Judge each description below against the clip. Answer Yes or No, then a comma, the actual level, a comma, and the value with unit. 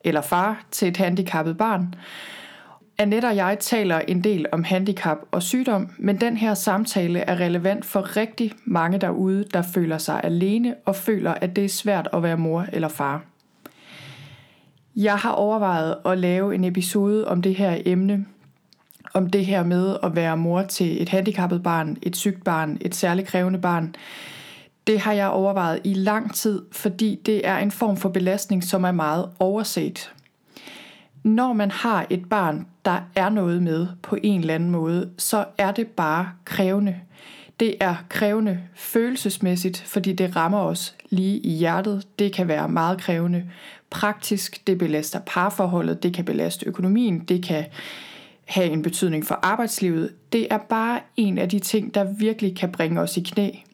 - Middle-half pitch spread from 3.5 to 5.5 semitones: No, average, 2.8 semitones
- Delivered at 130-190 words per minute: Yes, average, 170 wpm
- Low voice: No, high, 190 Hz